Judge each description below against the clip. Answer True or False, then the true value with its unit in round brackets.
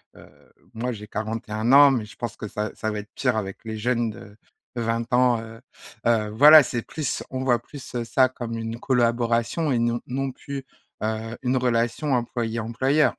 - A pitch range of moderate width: False (2.3 semitones)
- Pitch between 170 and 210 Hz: False (120 Hz)